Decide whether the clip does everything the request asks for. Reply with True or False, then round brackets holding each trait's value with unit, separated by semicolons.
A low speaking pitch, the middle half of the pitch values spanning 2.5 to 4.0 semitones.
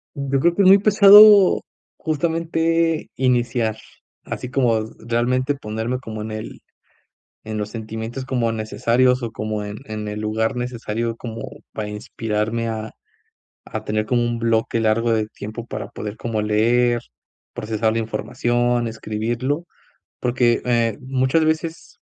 True (115 Hz; 2.8 semitones)